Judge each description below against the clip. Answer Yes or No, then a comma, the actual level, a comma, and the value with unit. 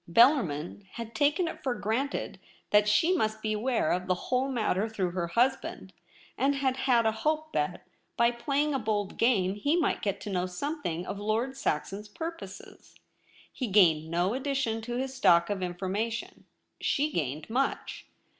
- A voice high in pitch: Yes, high, 225 Hz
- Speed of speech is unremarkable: Yes, average, 170 wpm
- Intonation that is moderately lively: No, wide, 5.9 semitones